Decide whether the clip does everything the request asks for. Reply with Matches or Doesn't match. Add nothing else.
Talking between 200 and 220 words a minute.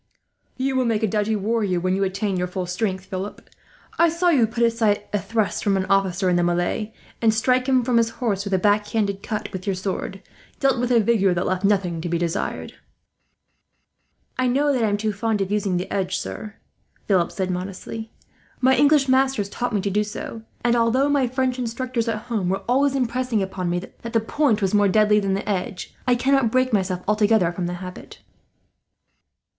Matches